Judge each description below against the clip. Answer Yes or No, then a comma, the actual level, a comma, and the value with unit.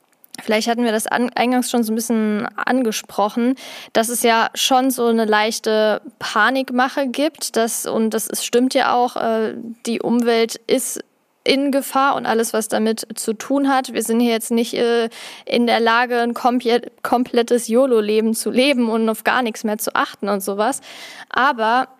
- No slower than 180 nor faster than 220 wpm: No, average, 165 wpm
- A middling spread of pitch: No, narrow, 2.2 semitones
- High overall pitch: Yes, high, 235 Hz